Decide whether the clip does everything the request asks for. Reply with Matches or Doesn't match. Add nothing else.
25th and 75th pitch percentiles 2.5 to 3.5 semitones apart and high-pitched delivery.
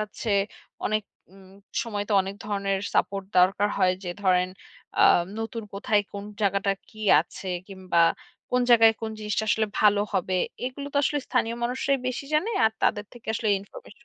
Matches